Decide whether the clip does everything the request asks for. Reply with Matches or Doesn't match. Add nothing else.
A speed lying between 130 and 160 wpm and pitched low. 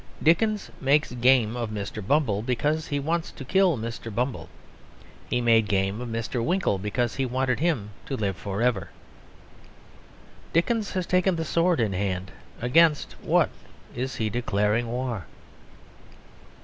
Matches